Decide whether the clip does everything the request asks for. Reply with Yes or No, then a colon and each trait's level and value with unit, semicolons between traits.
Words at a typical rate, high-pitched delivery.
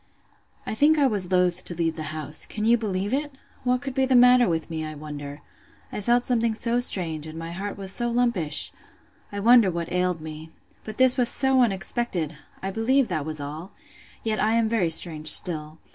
Yes: average, 180 wpm; high, 195 Hz